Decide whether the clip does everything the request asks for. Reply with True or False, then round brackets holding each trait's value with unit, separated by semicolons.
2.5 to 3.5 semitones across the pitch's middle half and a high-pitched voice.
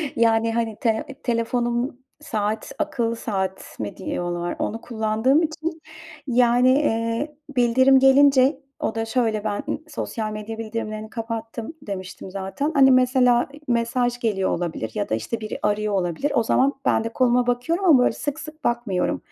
True (3.2 semitones; 230 Hz)